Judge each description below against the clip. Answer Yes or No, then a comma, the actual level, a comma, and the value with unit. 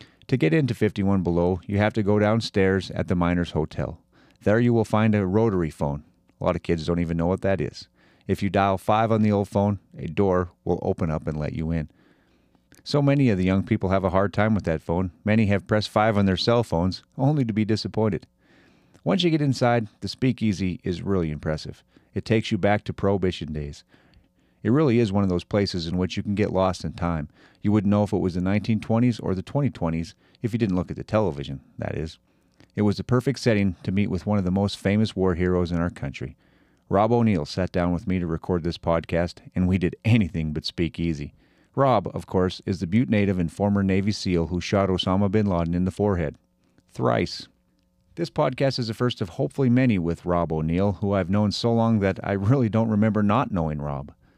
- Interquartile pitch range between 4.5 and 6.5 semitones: No, average, 3.7 semitones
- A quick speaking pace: Yes, fast, 225 wpm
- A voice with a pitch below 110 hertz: Yes, very low, 95 Hz